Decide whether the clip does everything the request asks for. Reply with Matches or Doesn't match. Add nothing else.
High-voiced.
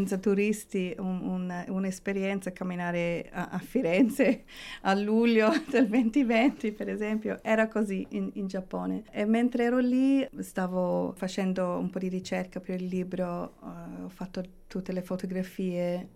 Matches